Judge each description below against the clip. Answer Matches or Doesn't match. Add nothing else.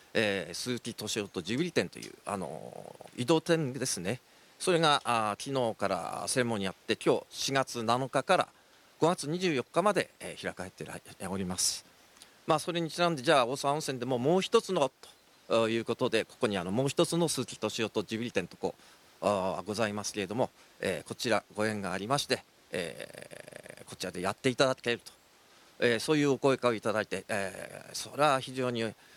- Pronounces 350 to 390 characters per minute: Matches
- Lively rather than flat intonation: Doesn't match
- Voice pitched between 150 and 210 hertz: Doesn't match